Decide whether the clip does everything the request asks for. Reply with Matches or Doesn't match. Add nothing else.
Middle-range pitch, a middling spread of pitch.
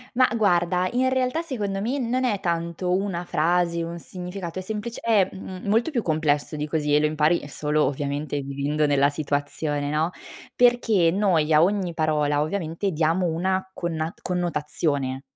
Matches